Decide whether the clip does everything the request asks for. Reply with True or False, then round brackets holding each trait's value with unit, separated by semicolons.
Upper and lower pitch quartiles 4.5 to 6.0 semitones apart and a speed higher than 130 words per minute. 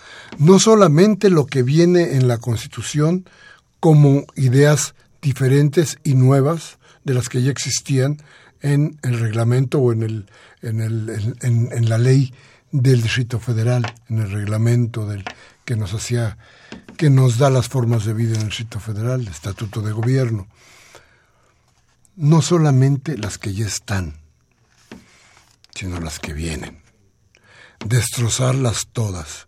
False (3.8 semitones; 140 wpm)